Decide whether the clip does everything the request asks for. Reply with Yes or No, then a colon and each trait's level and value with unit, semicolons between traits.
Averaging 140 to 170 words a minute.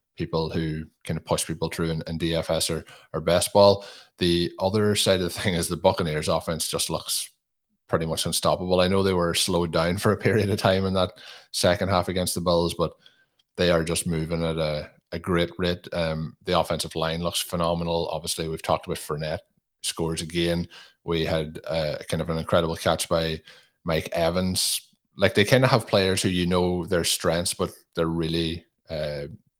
No: average, 195 wpm